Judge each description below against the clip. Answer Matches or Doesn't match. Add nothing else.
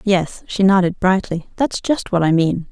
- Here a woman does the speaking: Matches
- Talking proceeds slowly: Doesn't match